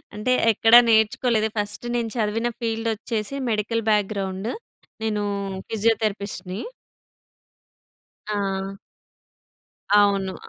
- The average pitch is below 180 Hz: No, high, 215 Hz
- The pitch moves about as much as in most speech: No, narrow, 2.0 semitones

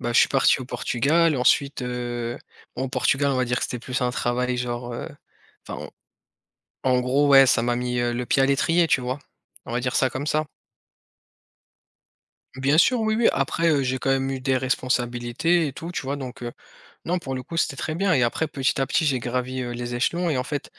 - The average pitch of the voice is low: Yes, low, 130 Hz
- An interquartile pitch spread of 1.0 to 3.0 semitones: Yes, narrow, 2.6 semitones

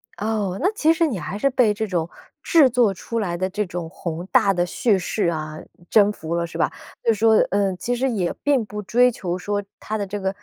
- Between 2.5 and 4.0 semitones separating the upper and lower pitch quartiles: No, average, 4.4 semitones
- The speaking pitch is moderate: No, high, 205 Hz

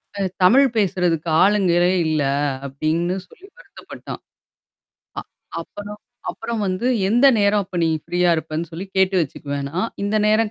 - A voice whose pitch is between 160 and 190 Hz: Yes, medium, 185 Hz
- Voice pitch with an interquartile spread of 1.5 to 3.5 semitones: No, average, 4.0 semitones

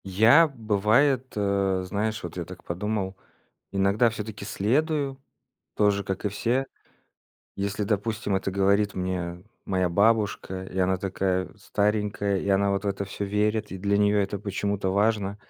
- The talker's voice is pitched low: Yes, low, 100 Hz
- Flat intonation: Yes, narrow, 1.8 semitones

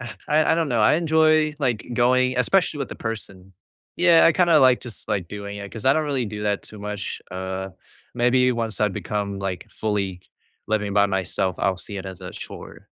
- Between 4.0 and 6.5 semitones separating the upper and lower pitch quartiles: Yes, average, 5.1 semitones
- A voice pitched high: No, low, 110 Hz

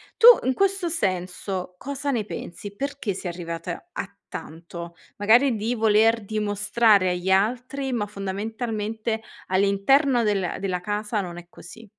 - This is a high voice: Yes, high, 210 Hz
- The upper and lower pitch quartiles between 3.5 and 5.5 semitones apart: Yes, average, 3.9 semitones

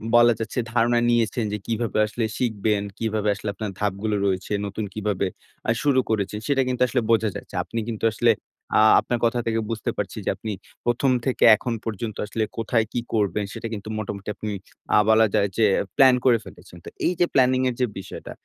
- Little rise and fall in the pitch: Yes, narrow, 2.3 semitones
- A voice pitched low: Yes, low, 110 Hz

